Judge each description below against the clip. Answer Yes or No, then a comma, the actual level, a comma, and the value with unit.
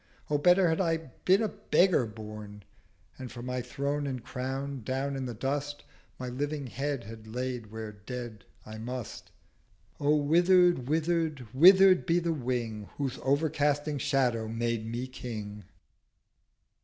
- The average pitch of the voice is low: Yes, low, 130 Hz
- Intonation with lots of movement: No, average, 4.1 semitones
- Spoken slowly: No, average, 145 wpm